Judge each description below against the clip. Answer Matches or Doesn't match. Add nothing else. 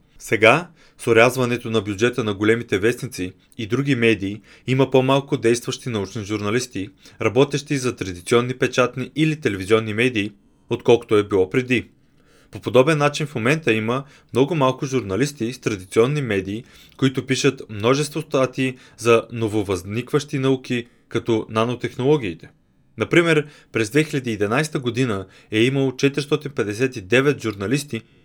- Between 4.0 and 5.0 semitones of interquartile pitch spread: Doesn't match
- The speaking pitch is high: Doesn't match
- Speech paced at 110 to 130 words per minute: Matches